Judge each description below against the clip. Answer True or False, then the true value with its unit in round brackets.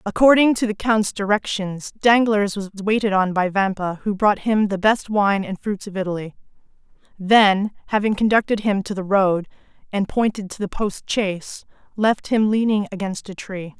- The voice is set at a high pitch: True (205 Hz)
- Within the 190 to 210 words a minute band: False (175 wpm)